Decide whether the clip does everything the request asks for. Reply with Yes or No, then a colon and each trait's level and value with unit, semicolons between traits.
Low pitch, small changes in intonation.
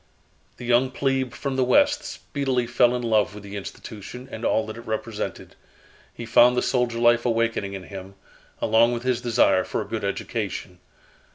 Yes: low, 120 Hz; narrow, 2.3 semitones